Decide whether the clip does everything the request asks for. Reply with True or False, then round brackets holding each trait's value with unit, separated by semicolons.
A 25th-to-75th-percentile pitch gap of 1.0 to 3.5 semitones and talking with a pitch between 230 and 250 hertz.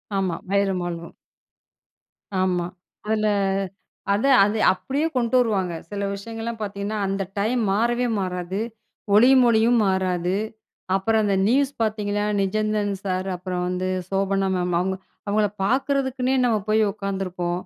False (3.1 semitones; 200 Hz)